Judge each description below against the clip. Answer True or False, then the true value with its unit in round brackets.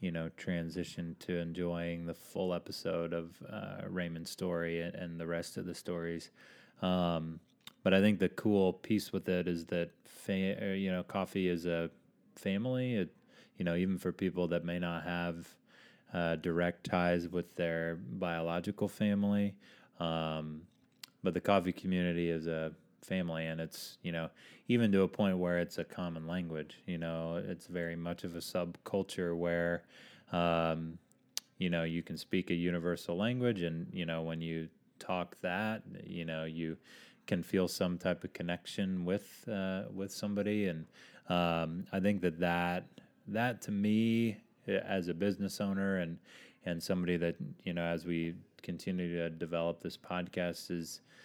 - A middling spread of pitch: False (2.0 semitones)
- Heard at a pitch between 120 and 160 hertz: False (85 Hz)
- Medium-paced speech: True (165 wpm)